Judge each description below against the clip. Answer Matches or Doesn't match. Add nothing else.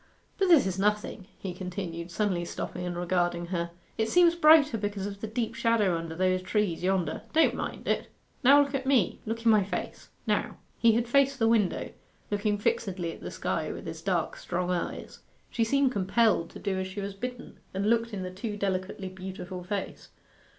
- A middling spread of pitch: Matches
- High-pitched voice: Matches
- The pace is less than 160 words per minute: Doesn't match